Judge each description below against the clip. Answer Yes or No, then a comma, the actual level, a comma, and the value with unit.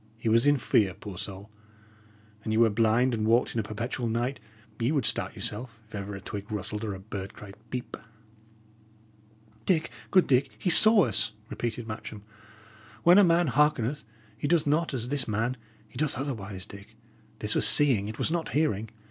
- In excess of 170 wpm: Yes, average, 185 wpm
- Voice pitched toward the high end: No, low, 115 Hz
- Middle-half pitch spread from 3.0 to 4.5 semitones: No, average, 4.9 semitones